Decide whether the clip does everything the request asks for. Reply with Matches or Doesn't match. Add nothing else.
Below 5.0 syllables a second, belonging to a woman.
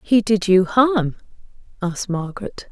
Matches